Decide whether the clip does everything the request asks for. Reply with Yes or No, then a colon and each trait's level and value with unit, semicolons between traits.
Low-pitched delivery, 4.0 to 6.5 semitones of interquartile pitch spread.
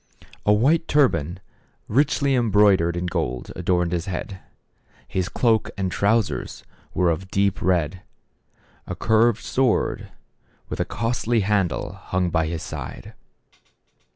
Yes: very low, 95 Hz; average, 4.5 semitones